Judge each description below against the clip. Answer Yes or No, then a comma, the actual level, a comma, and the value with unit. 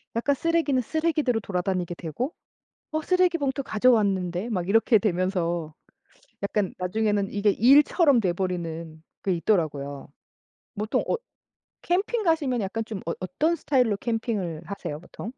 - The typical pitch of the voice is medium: No, high, 210 Hz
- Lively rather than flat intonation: Yes, wide, 6.9 semitones